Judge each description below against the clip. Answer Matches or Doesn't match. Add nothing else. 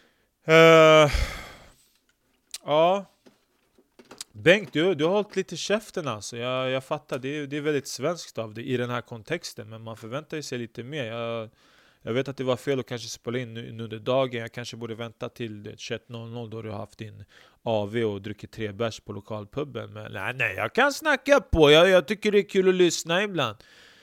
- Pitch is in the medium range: Doesn't match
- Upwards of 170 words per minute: Matches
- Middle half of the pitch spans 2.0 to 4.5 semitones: Doesn't match